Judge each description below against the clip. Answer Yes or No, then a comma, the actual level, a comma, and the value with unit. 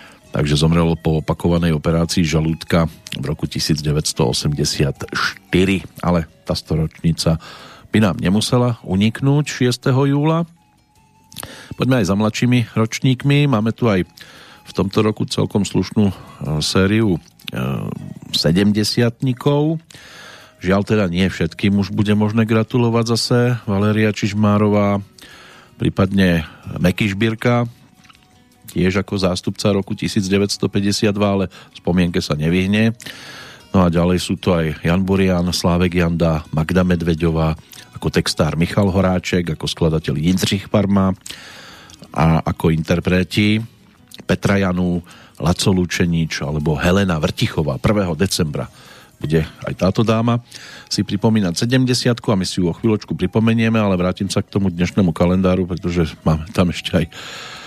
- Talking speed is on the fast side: No, average, 120 wpm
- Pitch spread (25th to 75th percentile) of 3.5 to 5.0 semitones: Yes, average, 4.1 semitones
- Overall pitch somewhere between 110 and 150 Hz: No, very low, 95 Hz